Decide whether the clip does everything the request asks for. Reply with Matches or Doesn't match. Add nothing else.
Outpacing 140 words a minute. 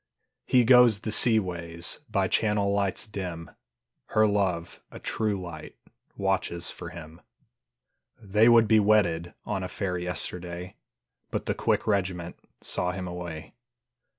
Doesn't match